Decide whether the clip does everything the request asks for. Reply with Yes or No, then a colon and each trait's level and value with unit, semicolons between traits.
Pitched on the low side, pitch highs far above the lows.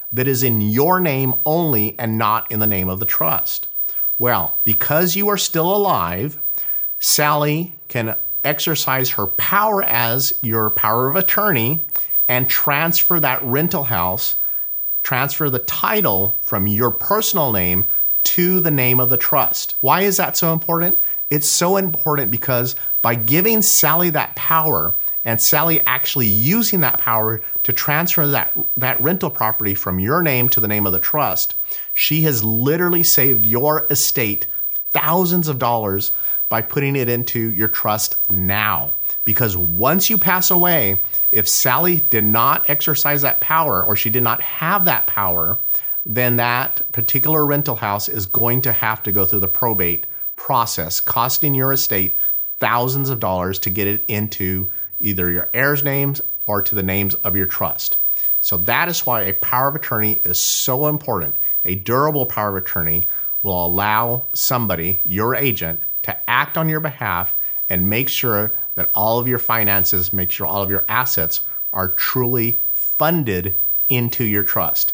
Yes: low, 120 Hz; wide, 6.4 semitones